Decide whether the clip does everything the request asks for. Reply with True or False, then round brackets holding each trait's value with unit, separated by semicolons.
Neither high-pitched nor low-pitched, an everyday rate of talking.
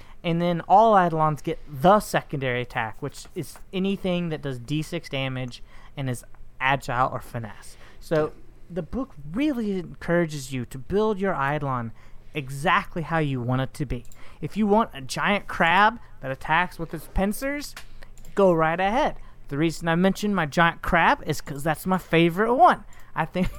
True (160 Hz; 170 wpm)